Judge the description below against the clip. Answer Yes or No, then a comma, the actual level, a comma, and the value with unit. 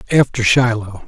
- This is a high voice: No, low, 120 Hz